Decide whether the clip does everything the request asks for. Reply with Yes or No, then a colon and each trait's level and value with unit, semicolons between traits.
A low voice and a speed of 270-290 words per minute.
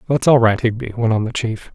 Yes: low, 115 Hz; fast, 275 wpm